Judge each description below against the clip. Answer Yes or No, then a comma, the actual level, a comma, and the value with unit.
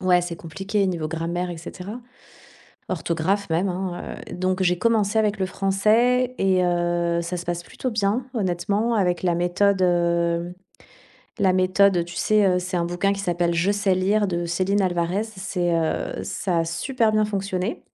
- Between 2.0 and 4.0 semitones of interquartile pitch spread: Yes, narrow, 2.6 semitones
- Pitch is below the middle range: No, medium, 185 Hz